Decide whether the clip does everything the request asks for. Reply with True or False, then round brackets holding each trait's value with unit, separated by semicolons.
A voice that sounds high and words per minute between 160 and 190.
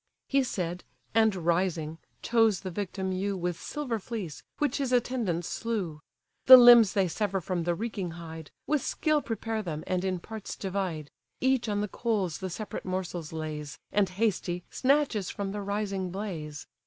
True (195 Hz; 165 wpm)